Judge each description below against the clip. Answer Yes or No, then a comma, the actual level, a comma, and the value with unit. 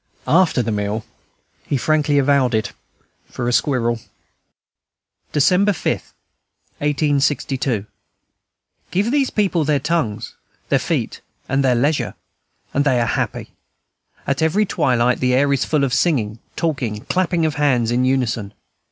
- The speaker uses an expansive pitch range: No, average, 4.3 semitones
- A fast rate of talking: No, slow, 135 wpm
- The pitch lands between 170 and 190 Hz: No, medium, 140 Hz